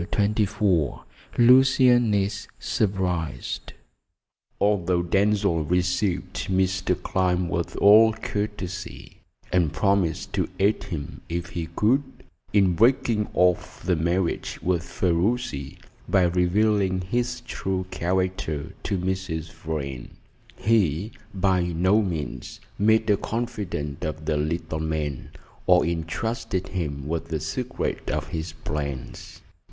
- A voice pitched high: No, very low, 90 Hz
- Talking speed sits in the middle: No, slow, 115 wpm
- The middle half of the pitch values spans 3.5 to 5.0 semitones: Yes, average, 3.9 semitones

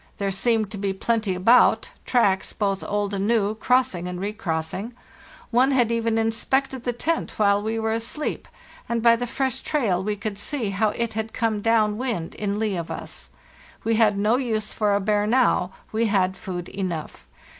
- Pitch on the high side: Yes, high, 215 Hz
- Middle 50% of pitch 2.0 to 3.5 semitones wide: Yes, average, 2.7 semitones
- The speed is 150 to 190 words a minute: Yes, average, 185 wpm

